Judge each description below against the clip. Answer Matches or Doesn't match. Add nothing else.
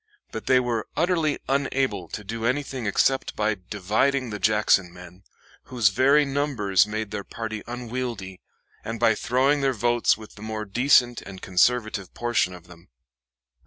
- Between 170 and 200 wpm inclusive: Doesn't match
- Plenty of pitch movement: Doesn't match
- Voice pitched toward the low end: Matches